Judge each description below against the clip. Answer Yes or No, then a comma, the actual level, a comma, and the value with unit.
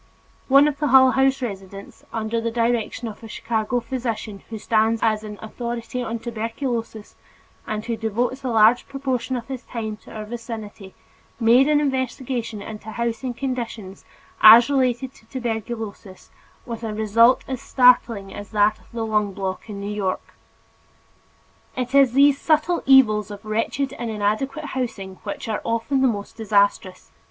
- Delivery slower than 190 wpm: Yes, average, 160 wpm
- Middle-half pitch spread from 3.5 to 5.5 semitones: No, average, 3.0 semitones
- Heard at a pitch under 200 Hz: No, high, 230 Hz